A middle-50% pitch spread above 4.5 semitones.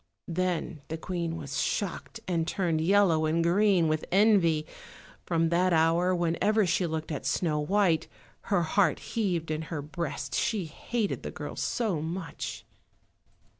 No: average, 3.0 semitones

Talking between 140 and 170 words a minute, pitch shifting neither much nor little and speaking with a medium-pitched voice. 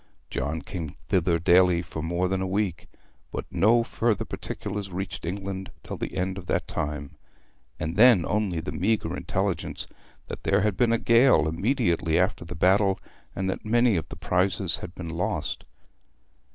No: average, 165 wpm; average, 3.5 semitones; very low, 95 Hz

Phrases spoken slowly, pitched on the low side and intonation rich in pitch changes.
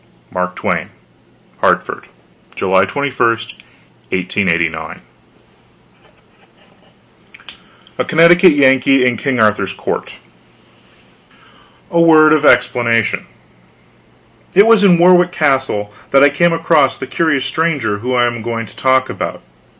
Yes: slow, 110 wpm; low, 130 Hz; wide, 6.3 semitones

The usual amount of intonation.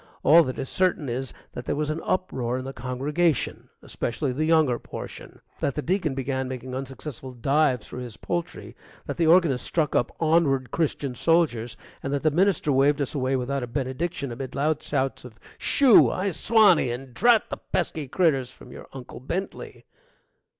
Yes: average, 4.1 semitones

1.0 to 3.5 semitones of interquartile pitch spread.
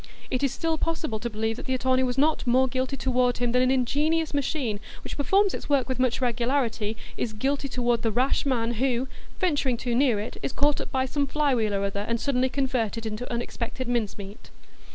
Yes: average, 2.9 semitones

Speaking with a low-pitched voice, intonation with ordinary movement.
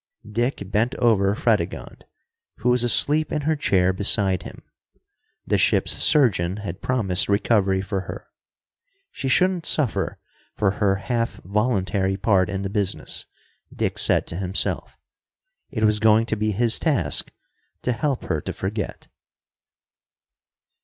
Yes: low, 105 Hz; average, 4.0 semitones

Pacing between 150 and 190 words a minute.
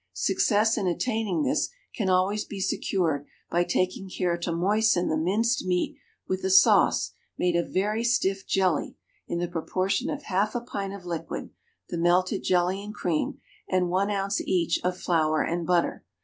Yes: average, 170 wpm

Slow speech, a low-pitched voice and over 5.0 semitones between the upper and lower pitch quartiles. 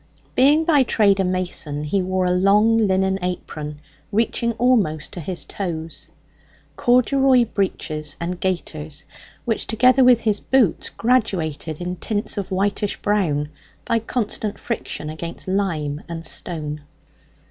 No: slow, 130 wpm; high, 190 Hz; wide, 5.6 semitones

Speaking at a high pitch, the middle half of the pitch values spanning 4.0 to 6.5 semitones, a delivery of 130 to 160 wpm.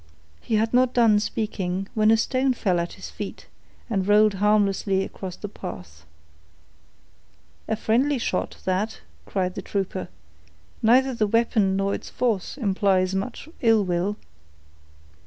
No: high, 205 Hz; average, 3.0 semitones; average, 140 wpm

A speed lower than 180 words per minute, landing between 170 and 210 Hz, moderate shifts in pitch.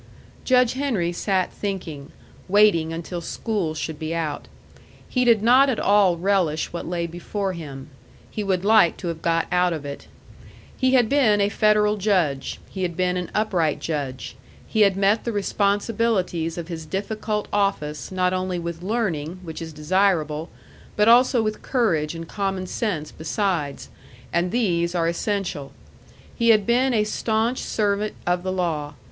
Yes: average, 160 wpm; medium, 185 Hz; average, 4.3 semitones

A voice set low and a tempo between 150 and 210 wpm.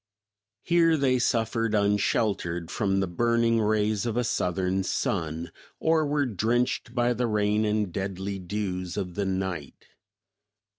No: low, 105 Hz; slow, 135 wpm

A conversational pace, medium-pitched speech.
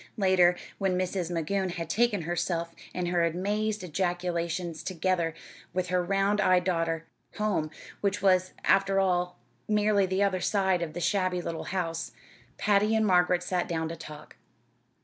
Yes: average, 150 wpm; medium, 180 Hz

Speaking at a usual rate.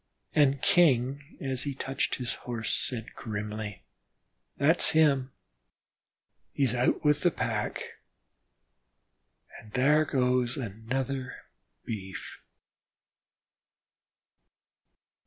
No: slow, 85 wpm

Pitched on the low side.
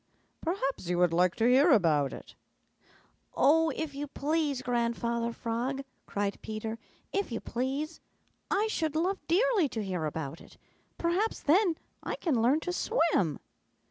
No: very high, 265 Hz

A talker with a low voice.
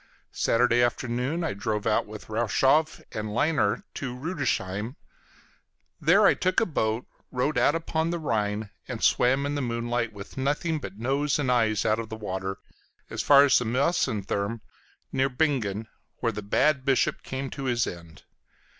Yes: low, 125 Hz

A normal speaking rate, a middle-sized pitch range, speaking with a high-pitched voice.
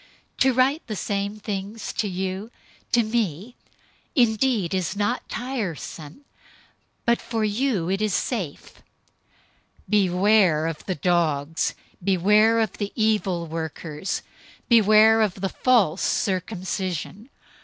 No: slow, 115 wpm; average, 3.6 semitones; high, 205 Hz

